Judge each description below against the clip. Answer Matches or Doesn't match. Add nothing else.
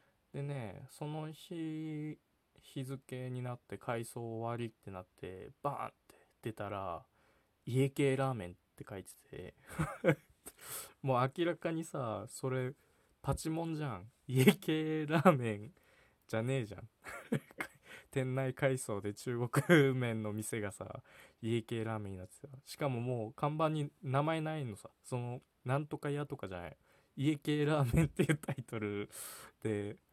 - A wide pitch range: Doesn't match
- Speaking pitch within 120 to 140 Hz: Matches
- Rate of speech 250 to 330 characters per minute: Matches